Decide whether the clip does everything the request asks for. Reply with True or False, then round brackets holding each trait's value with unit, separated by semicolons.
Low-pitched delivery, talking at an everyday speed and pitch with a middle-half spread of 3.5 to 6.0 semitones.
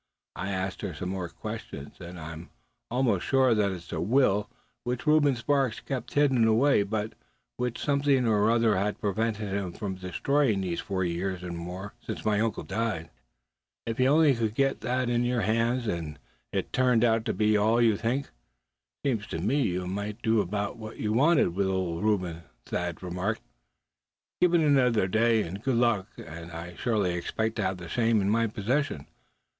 True (110 Hz; 180 wpm; 4.5 semitones)